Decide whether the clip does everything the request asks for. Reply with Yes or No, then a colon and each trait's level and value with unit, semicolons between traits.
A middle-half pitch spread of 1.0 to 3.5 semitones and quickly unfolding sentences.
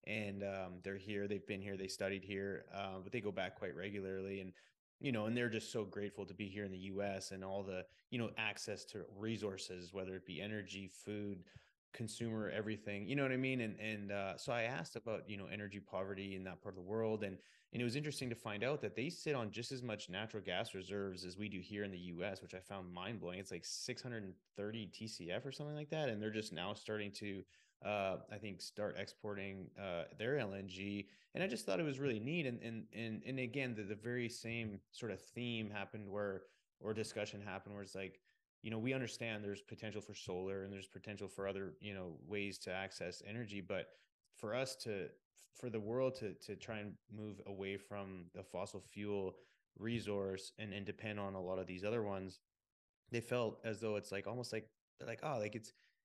Yes: narrow, 2.4 semitones; fast, 225 wpm